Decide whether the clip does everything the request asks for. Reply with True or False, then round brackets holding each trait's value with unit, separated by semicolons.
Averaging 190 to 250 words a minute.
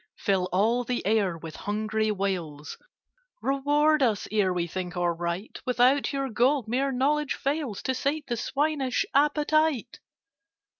False (140 wpm)